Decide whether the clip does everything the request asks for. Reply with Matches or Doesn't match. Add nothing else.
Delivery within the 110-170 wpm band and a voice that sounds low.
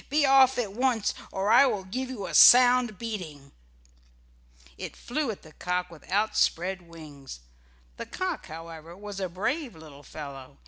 Doesn't match